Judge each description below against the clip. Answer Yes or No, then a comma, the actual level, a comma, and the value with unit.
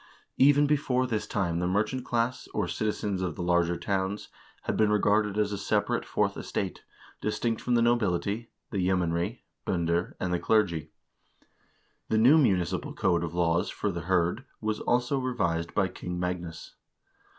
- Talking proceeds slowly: No, average, 160 wpm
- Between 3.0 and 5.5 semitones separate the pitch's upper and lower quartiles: Yes, average, 4.6 semitones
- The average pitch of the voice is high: No, low, 100 Hz